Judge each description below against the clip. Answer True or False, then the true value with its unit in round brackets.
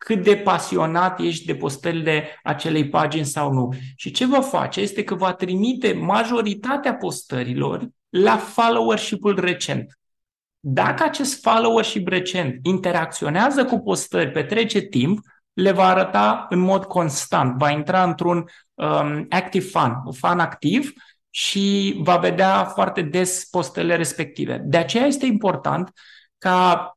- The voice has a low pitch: False (185 Hz)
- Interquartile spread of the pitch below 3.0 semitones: False (4.4 semitones)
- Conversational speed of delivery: True (135 wpm)